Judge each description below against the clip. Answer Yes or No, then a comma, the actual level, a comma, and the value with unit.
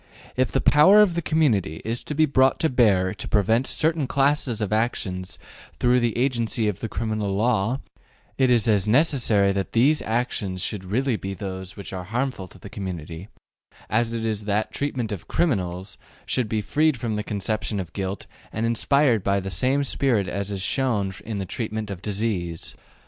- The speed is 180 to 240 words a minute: Yes, average, 185 wpm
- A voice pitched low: Yes, low, 110 Hz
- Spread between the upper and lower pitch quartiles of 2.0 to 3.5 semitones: No, average, 4.7 semitones